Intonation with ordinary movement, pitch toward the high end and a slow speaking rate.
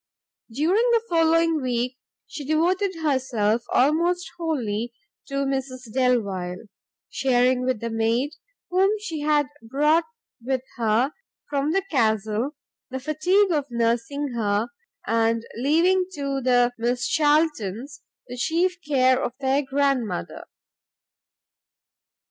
Yes: average, 4.8 semitones; very high, 265 Hz; slow, 115 wpm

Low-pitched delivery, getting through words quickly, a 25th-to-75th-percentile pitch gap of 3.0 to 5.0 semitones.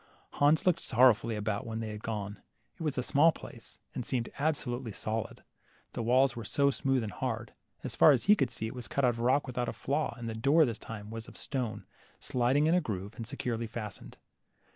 Yes: low, 120 Hz; fast, 220 wpm; average, 3.7 semitones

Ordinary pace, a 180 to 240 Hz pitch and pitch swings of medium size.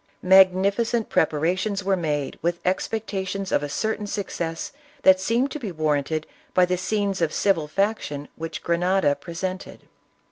Yes: average, 145 wpm; medium, 185 Hz; average, 3.6 semitones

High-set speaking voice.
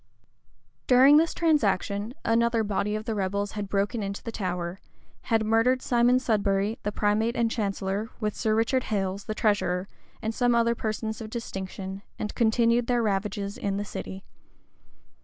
Yes: high, 215 Hz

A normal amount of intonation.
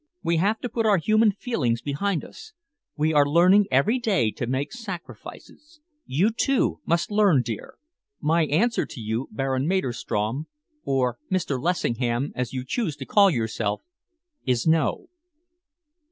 No: wide, 8.0 semitones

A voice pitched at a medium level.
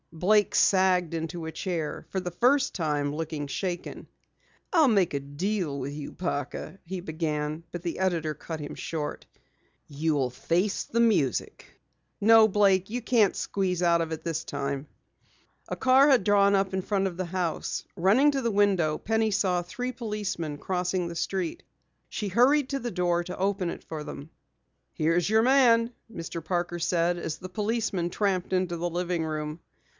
Yes: medium, 180 Hz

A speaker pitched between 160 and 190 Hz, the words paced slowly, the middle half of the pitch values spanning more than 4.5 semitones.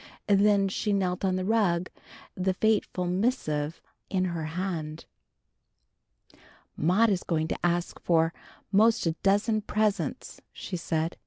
No: medium, 185 Hz; slow, 130 wpm; average, 3.3 semitones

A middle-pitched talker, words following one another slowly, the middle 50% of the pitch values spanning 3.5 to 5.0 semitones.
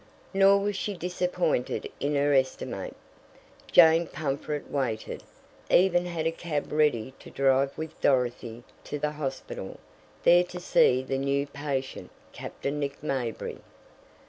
Yes: medium, 145 Hz; slow, 130 wpm; average, 4.2 semitones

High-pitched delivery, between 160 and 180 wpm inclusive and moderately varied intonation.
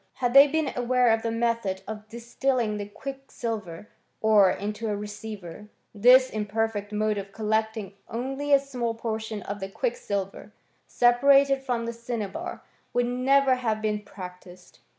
No: high, 225 Hz; average, 145 wpm; average, 3.2 semitones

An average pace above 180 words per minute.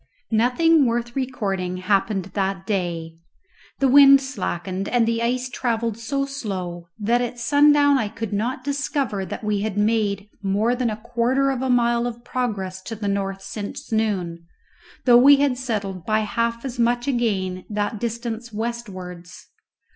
No: average, 155 wpm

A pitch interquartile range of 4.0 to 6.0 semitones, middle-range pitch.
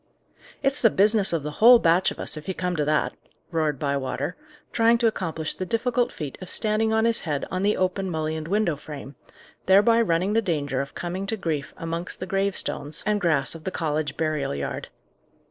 Yes: wide, 5.4 semitones; medium, 175 Hz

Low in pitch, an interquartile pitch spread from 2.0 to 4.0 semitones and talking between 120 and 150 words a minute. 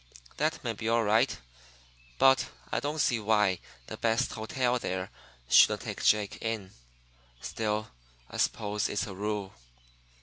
Yes: low, 110 Hz; narrow, 2.6 semitones; average, 140 wpm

